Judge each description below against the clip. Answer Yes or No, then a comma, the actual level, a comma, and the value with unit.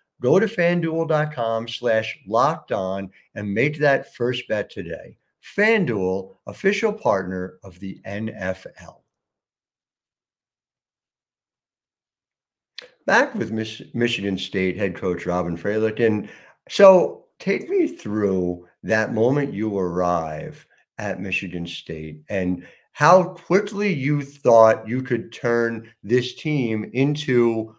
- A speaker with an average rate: No, slow, 105 wpm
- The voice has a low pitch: Yes, low, 110 Hz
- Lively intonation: Yes, wide, 7.0 semitones